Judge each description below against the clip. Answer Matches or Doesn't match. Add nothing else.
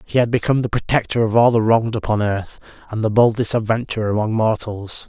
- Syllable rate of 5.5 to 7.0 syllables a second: Matches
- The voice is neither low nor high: Doesn't match